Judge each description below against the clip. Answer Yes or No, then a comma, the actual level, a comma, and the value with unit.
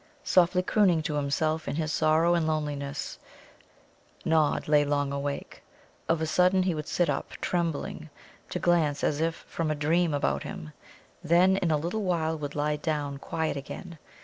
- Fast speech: No, average, 170 wpm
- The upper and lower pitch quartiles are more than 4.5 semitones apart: No, narrow, 2.6 semitones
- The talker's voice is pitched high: No, medium, 155 Hz